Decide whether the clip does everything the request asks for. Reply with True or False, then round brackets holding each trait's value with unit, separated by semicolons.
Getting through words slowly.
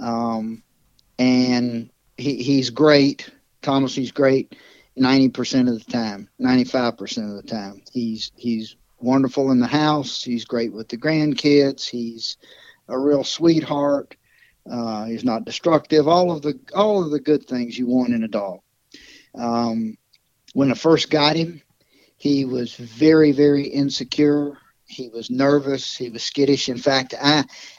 False (150 wpm)